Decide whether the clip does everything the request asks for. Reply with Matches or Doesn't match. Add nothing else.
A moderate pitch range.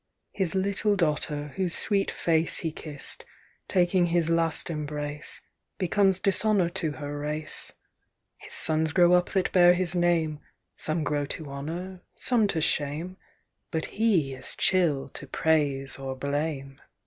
Matches